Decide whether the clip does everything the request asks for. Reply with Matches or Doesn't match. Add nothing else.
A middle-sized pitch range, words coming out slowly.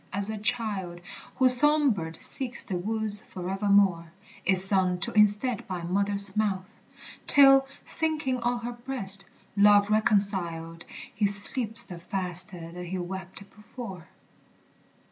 Matches